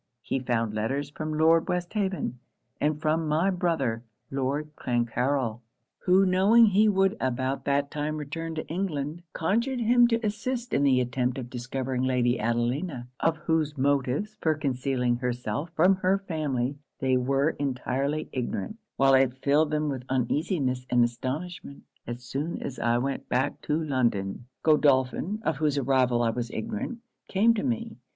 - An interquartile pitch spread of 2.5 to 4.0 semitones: No, average, 4.7 semitones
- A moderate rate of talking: Yes, average, 155 wpm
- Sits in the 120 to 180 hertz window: Yes, medium, 140 Hz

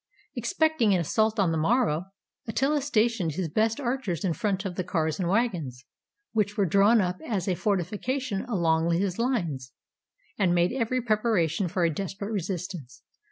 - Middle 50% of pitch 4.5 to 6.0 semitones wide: Yes, average, 4.9 semitones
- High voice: Yes, high, 195 Hz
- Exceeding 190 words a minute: No, average, 160 wpm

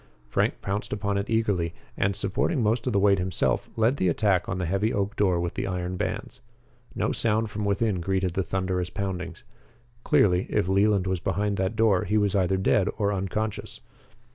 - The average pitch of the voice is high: No, low, 100 Hz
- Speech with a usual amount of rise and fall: No, narrow, 2.2 semitones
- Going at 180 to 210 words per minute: Yes, average, 190 wpm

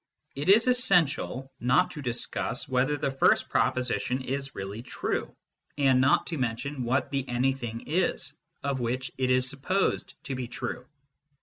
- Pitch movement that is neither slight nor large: No, narrow, 2.2 semitones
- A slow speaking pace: No, average, 150 wpm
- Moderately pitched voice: No, low, 130 Hz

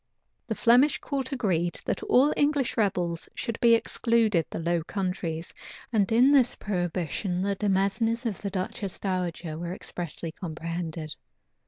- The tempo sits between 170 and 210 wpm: No, average, 140 wpm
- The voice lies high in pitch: Yes, high, 195 Hz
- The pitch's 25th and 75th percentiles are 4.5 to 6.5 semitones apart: Yes, average, 5.1 semitones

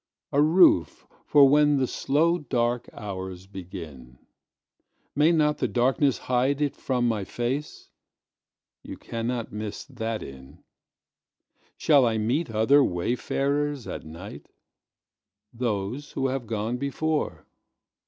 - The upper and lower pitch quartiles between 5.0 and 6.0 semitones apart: Yes, average, 5.3 semitones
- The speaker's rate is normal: No, slow, 105 wpm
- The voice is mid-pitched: No, low, 125 Hz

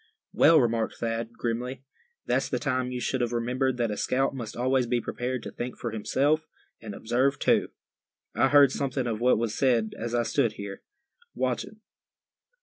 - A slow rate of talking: No, average, 175 wpm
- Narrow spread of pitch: Yes, narrow, 2.2 semitones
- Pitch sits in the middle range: No, low, 120 Hz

